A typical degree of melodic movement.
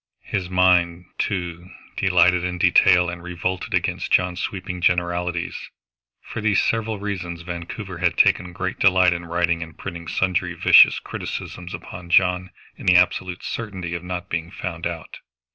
No: narrow, 1.2 semitones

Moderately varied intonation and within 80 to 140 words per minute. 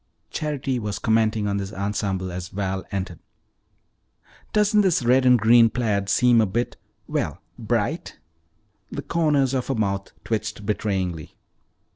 Yes: average, 4.2 semitones; slow, 135 wpm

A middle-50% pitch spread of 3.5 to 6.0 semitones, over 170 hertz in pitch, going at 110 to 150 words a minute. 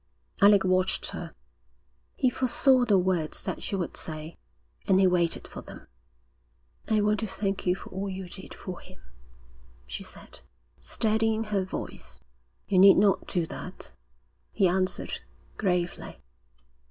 No: average, 2.8 semitones; high, 190 Hz; average, 140 wpm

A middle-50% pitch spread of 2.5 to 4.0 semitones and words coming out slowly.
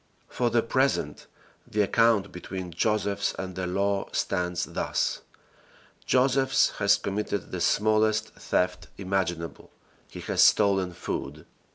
Yes: average, 2.8 semitones; slow, 115 wpm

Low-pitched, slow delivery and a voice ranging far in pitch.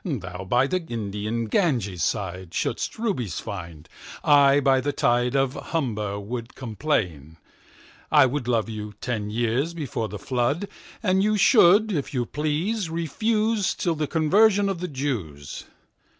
Yes: low, 130 Hz; slow, 125 wpm; wide, 7.9 semitones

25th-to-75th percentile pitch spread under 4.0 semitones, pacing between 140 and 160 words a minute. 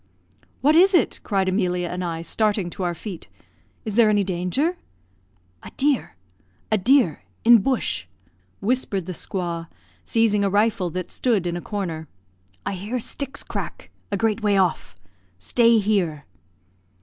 No: average, 4.3 semitones; average, 150 wpm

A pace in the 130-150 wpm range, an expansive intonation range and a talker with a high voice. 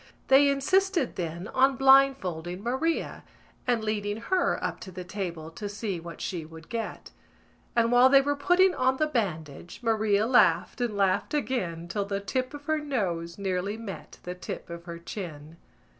No: average, 175 wpm; wide, 7.2 semitones; high, 210 Hz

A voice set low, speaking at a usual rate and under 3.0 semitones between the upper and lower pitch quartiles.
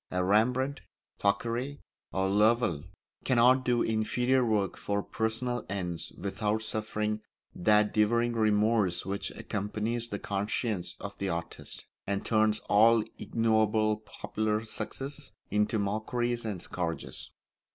No: low, 110 Hz; slow, 115 wpm; narrow, 2.5 semitones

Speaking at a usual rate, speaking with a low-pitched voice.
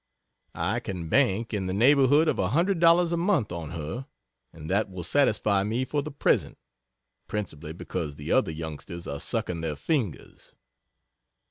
Yes: average, 150 wpm; low, 100 Hz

